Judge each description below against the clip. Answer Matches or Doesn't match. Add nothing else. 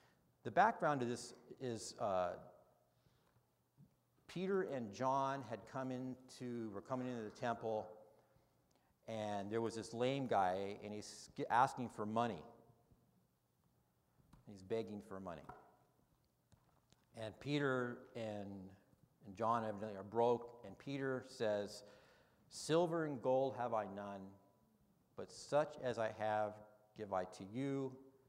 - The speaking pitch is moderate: Doesn't match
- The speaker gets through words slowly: Matches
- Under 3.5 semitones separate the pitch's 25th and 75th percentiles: Doesn't match